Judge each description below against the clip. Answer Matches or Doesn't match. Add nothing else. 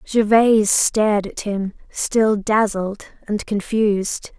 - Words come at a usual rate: Doesn't match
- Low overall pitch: Doesn't match